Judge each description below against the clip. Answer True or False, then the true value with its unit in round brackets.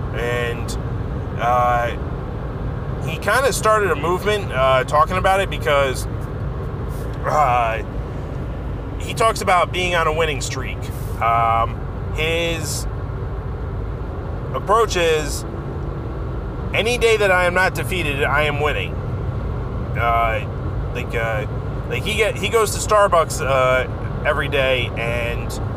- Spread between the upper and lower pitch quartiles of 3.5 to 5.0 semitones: False (2.9 semitones)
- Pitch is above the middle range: False (120 Hz)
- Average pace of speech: False (115 wpm)